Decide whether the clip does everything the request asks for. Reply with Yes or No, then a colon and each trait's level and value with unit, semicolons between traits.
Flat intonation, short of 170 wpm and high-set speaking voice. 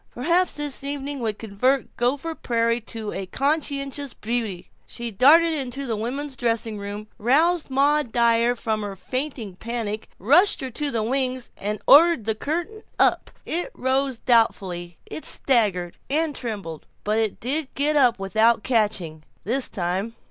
No: average, 4.6 semitones; average, 150 wpm; high, 240 Hz